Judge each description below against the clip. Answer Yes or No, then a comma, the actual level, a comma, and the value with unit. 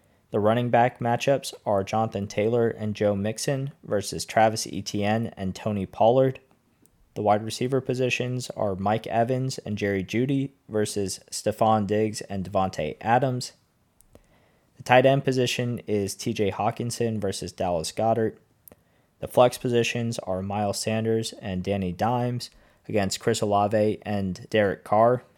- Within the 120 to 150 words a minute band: Yes, slow, 135 wpm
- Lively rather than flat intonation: No, average, 3.1 semitones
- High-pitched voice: No, low, 110 Hz